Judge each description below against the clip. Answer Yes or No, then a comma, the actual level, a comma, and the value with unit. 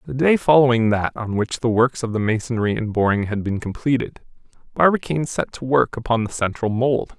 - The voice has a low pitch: Yes, low, 120 Hz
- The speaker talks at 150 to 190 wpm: No, average, 200 wpm